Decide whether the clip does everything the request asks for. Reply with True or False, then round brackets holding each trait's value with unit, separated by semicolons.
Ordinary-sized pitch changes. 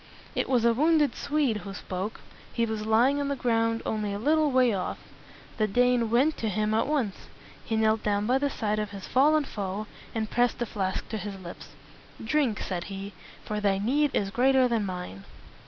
True (4.0 semitones)